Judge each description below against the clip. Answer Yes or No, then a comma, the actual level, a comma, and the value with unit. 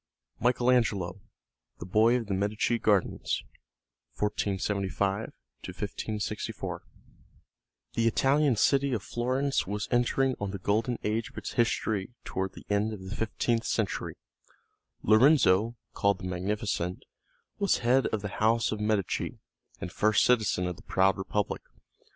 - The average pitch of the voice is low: Yes, low, 105 Hz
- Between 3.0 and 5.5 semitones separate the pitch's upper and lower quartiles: Yes, average, 3.3 semitones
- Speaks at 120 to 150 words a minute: Yes, slow, 135 wpm